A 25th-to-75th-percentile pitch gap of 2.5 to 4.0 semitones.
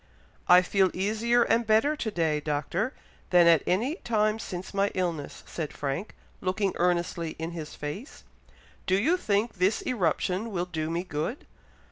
No: average, 4.6 semitones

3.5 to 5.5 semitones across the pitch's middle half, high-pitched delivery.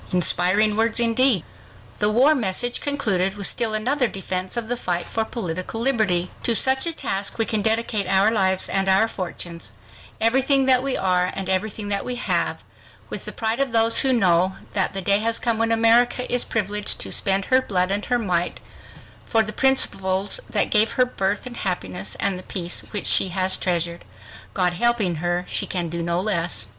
Yes: average, 4.0 semitones; high, 205 Hz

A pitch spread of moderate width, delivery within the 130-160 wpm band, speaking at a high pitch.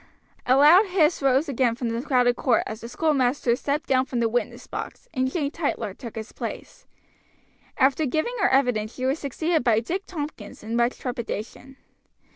No: average, 3.9 semitones; average, 180 wpm; very high, 260 Hz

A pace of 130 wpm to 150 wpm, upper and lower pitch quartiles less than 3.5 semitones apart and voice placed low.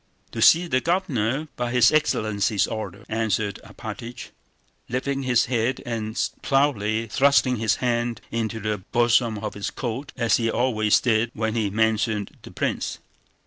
Yes: average, 145 wpm; narrow, 2.6 semitones; low, 115 Hz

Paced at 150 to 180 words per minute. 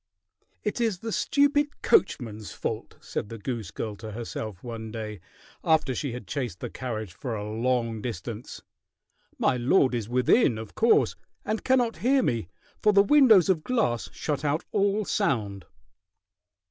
Yes: average, 155 wpm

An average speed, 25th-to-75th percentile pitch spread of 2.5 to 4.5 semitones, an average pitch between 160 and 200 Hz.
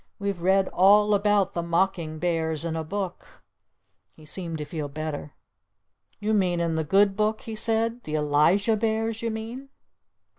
No: average, 160 wpm; average, 4.9 semitones; high, 190 Hz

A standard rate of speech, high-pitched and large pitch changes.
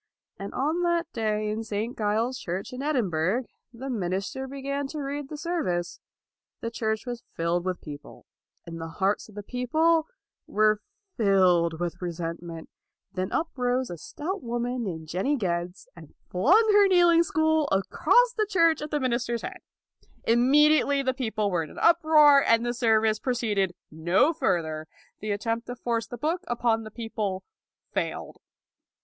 Yes: average, 165 wpm; high, 230 Hz; wide, 7.0 semitones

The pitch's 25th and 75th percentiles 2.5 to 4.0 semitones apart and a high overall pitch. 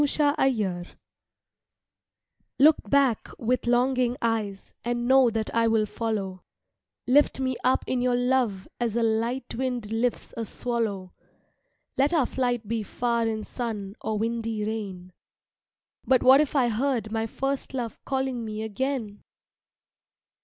Yes: average, 3.0 semitones; high, 235 Hz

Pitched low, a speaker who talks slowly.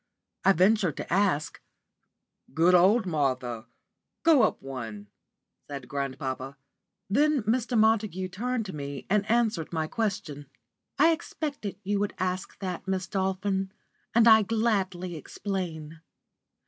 No: high, 190 Hz; slow, 120 wpm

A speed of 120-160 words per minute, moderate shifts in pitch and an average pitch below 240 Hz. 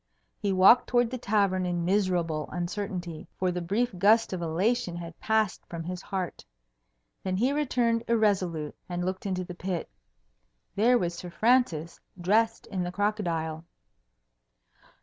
Yes: average, 145 wpm; average, 4.0 semitones; medium, 185 Hz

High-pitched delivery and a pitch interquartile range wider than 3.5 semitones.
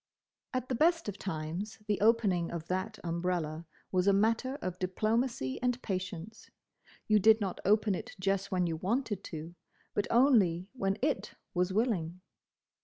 Yes: high, 195 Hz; average, 4.1 semitones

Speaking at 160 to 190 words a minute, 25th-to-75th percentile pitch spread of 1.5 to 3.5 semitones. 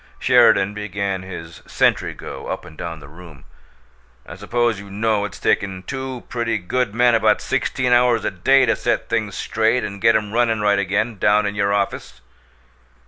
Yes: average, 180 wpm; average, 3.2 semitones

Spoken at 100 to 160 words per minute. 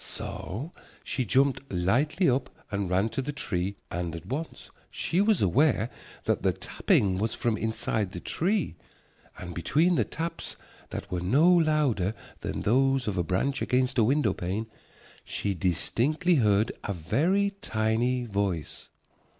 Yes: average, 150 wpm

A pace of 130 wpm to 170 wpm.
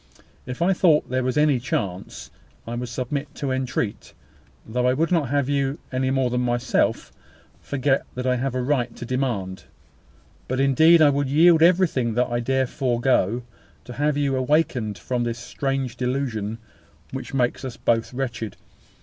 Yes: average, 165 wpm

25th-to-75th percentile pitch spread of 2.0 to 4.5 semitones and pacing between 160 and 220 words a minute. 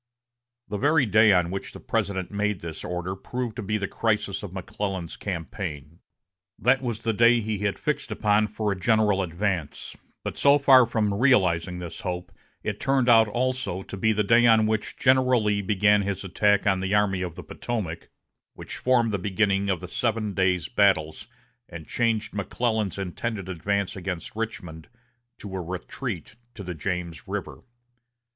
Yes: average, 3.4 semitones; average, 170 wpm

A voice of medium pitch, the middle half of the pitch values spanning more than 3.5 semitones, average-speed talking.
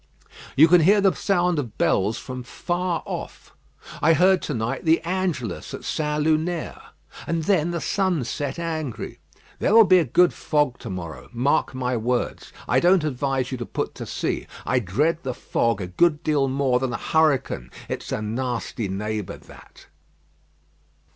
Yes: medium, 145 Hz; wide, 5.5 semitones; average, 170 wpm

